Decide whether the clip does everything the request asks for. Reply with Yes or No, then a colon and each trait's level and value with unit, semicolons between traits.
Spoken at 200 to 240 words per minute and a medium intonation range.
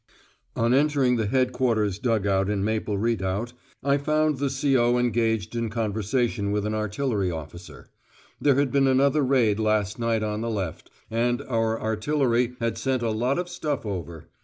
No: average, 165 wpm; average, 3.7 semitones